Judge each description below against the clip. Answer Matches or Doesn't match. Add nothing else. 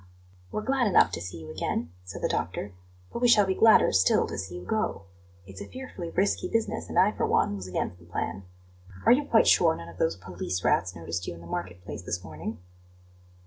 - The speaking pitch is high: Doesn't match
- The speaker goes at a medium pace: Doesn't match